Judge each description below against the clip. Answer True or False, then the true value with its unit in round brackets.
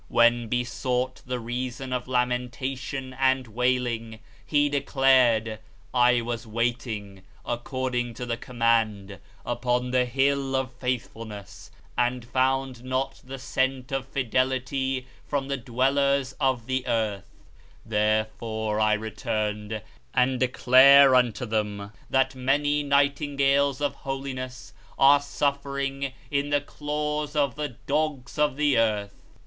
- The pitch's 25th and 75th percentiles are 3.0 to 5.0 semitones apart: False (2.6 semitones)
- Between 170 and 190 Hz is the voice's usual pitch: False (130 Hz)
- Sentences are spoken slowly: True (120 wpm)